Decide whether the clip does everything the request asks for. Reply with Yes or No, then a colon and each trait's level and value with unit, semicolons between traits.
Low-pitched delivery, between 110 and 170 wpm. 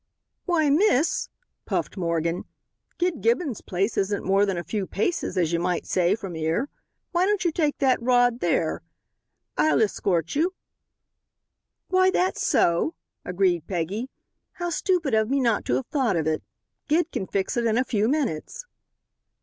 No: high, 220 Hz; average, 160 wpm